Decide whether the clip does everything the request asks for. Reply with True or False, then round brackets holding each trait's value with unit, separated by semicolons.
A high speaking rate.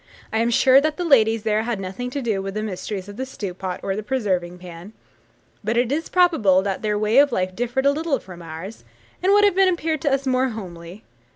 True (230 wpm)